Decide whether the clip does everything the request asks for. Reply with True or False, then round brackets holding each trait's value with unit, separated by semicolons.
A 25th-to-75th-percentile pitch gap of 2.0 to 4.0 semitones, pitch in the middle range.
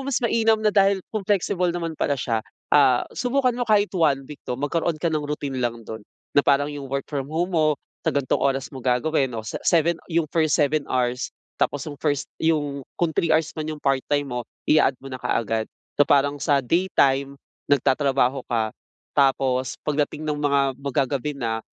True (3.3 semitones; 145 Hz)